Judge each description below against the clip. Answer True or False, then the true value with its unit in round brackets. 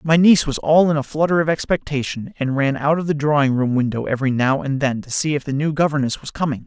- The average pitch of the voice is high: False (145 Hz)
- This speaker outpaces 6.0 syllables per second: True (6.3 syllables/s)